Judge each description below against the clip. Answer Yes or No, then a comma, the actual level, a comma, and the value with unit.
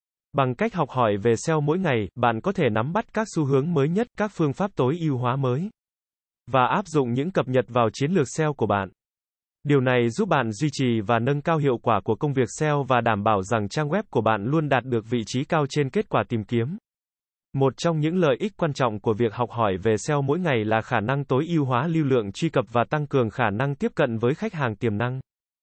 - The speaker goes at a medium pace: No, fast, 255 wpm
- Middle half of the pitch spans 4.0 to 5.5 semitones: Yes, average, 5.0 semitones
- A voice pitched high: No, low, 135 Hz